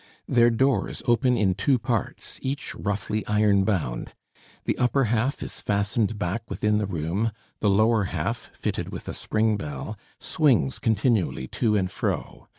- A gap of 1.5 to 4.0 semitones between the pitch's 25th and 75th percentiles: Yes, average, 3.1 semitones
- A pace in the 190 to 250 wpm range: No, average, 155 wpm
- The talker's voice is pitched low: Yes, low, 105 Hz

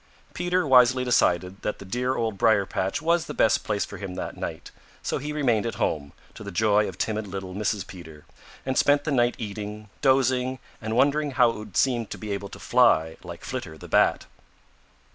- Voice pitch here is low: Yes, low, 110 Hz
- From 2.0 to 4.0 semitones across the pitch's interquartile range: No, average, 4.7 semitones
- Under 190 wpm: No, average, 200 wpm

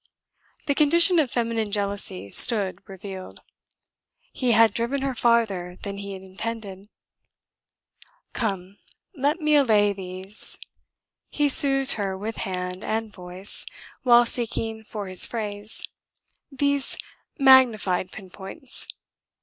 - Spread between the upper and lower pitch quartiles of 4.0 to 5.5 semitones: Yes, average, 4.8 semitones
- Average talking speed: No, slow, 110 wpm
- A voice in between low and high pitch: No, high, 215 Hz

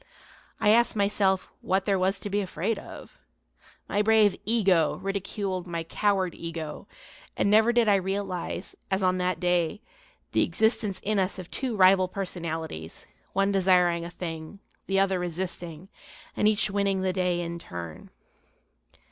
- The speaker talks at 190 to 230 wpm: No, average, 150 wpm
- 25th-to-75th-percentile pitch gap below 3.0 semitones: Yes, narrow, 2.5 semitones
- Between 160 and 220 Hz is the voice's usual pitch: Yes, high, 190 Hz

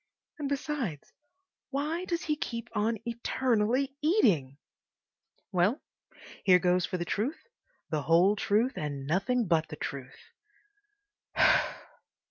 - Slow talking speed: Yes, slow, 110 wpm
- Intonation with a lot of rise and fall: Yes, wide, 8.0 semitones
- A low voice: No, high, 210 Hz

